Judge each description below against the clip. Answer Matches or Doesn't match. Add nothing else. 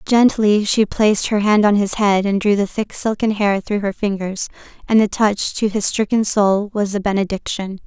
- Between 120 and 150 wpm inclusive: Doesn't match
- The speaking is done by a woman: Matches